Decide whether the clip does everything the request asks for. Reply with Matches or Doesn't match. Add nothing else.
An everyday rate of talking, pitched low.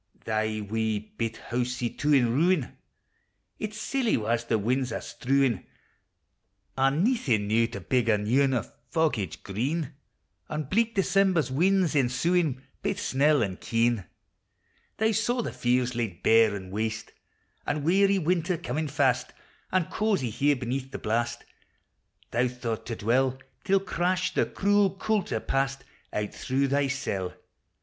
Matches